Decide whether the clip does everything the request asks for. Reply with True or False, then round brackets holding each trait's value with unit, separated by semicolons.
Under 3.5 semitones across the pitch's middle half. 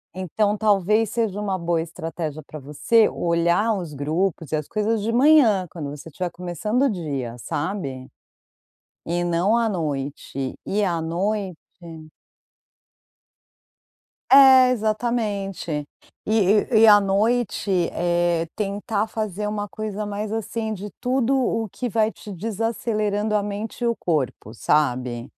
False (4.7 semitones)